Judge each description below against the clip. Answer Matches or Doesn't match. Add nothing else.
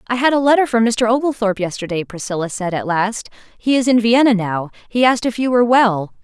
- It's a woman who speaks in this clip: Matches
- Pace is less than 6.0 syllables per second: Doesn't match